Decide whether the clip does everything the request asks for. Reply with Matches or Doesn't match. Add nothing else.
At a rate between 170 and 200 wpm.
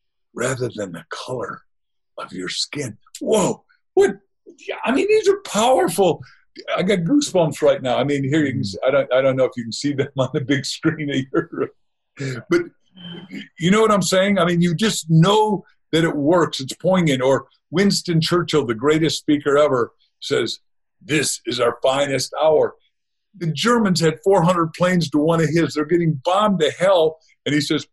Matches